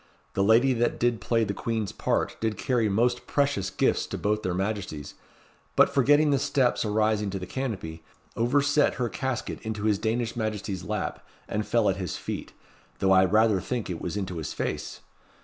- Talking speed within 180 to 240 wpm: Yes, average, 185 wpm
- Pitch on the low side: Yes, low, 110 Hz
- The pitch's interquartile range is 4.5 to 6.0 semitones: No, average, 3.8 semitones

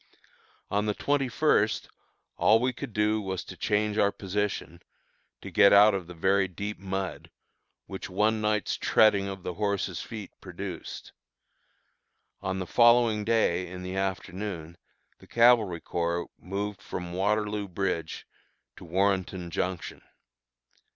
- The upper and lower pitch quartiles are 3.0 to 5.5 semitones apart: No, narrow, 2.5 semitones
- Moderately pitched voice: No, low, 100 Hz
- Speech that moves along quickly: No, slow, 135 wpm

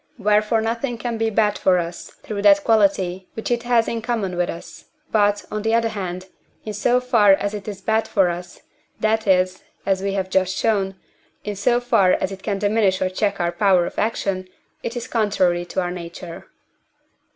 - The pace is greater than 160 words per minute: Yes, average, 195 wpm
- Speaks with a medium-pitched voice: No, high, 200 Hz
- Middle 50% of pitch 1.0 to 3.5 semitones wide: Yes, average, 3.0 semitones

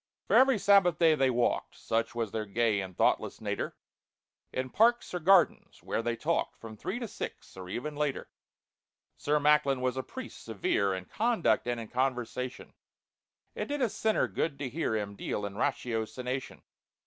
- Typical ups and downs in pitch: No, wide, 6.8 semitones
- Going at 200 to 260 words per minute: No, average, 170 wpm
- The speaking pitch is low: Yes, low, 130 Hz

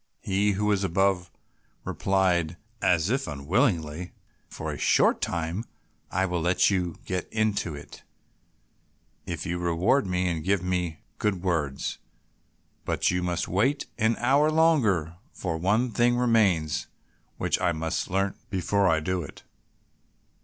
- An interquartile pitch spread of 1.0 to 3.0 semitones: No, average, 3.4 semitones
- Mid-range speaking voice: No, very low, 90 Hz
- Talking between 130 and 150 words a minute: Yes, average, 140 wpm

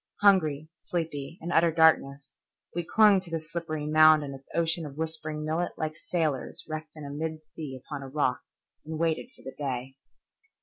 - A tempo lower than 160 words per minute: No, average, 175 wpm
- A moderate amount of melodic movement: No, narrow, 2.1 semitones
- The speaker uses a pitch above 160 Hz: No, medium, 155 Hz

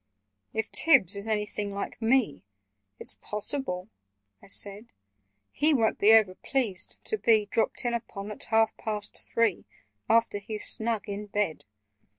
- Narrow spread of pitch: Yes, narrow, 2.3 semitones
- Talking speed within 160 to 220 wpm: No, average, 145 wpm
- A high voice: Yes, high, 215 Hz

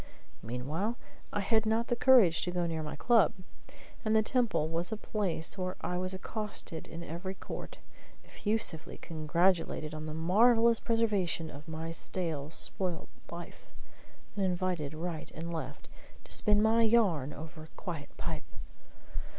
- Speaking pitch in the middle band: Yes, medium, 180 Hz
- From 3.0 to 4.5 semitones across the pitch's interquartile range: No, average, 5.1 semitones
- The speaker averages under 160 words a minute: Yes, average, 150 wpm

